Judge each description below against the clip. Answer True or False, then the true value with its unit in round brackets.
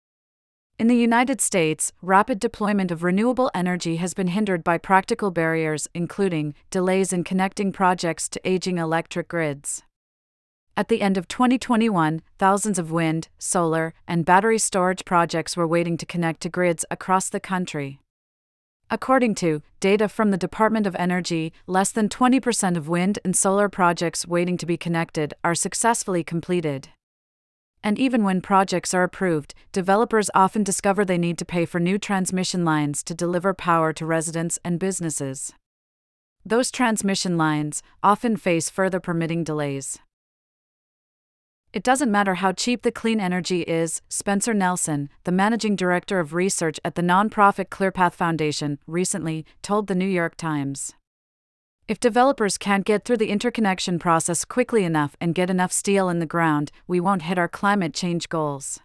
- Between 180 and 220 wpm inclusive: False (155 wpm)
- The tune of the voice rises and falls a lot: False (3.3 semitones)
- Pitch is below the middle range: False (180 Hz)